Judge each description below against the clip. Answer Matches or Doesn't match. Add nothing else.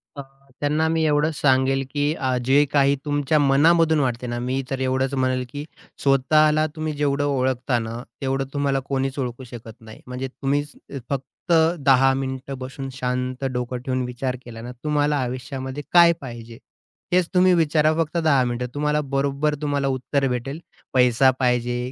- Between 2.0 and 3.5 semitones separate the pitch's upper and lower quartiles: Matches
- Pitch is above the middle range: Doesn't match